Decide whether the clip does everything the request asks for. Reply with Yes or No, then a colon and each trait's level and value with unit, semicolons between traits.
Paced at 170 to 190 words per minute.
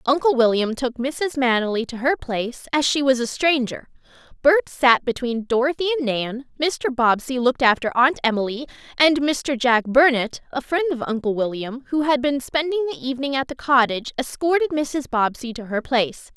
Yes: average, 180 wpm